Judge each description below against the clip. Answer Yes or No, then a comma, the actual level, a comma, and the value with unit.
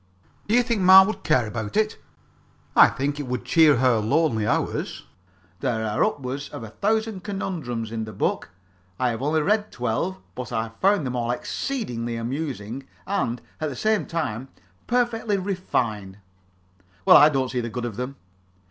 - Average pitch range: No, wide, 8.3 semitones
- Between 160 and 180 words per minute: Yes, average, 170 wpm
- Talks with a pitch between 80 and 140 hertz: Yes, low, 135 Hz